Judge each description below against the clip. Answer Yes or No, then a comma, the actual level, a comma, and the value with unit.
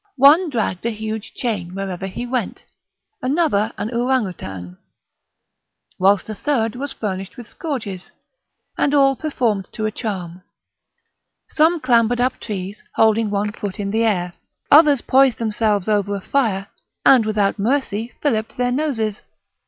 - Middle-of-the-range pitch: No, high, 220 Hz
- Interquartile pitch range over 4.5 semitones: No, average, 4.2 semitones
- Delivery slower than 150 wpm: Yes, average, 140 wpm